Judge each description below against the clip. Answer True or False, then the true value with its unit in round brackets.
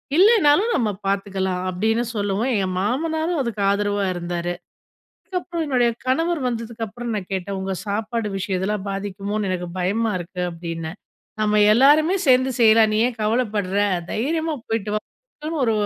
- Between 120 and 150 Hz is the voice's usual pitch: False (215 Hz)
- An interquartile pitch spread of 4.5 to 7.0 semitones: True (5.0 semitones)